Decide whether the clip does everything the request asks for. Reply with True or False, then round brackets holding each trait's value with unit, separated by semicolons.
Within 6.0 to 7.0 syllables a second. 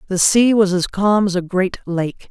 False (4.4 syllables/s)